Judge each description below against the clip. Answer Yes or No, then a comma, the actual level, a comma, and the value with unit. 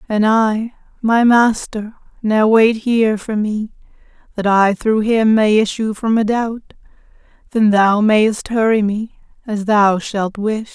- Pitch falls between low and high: No, high, 215 Hz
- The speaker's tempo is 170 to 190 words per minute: No, average, 150 wpm